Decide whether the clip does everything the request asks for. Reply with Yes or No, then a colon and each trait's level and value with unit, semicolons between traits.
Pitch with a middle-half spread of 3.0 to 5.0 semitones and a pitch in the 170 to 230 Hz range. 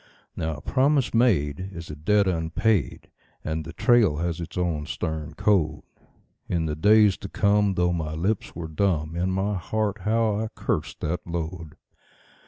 No: average, 4.6 semitones; very low, 90 Hz